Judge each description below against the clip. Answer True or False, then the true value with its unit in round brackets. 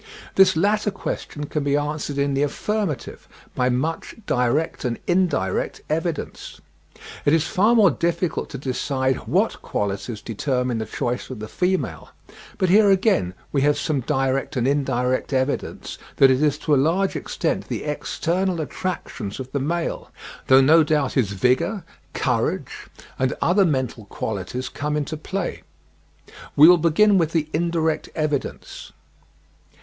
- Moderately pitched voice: True (150 Hz)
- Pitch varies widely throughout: False (4.7 semitones)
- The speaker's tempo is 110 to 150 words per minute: True (145 wpm)